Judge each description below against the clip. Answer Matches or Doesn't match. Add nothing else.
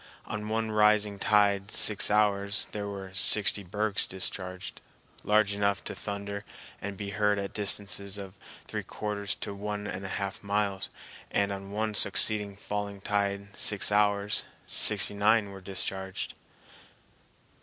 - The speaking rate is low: Doesn't match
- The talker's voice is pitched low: Matches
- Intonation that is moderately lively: Doesn't match